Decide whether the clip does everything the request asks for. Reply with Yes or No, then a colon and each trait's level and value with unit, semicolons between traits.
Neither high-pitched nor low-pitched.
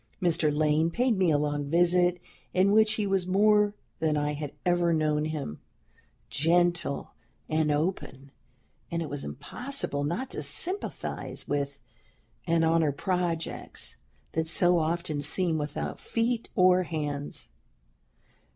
Yes: medium, 165 Hz